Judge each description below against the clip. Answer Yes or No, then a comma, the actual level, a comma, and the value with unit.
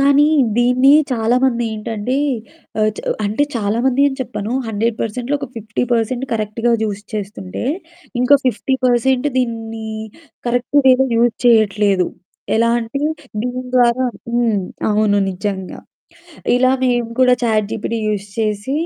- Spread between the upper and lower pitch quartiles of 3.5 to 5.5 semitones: No, average, 2.9 semitones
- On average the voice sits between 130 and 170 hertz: No, high, 230 Hz